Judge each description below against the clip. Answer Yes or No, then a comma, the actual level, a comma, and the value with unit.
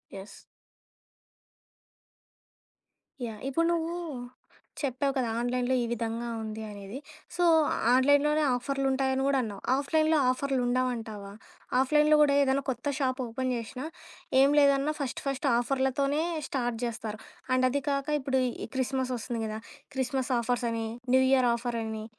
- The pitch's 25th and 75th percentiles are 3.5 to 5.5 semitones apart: No, average, 2.7 semitones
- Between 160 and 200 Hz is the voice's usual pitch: No, very high, 260 Hz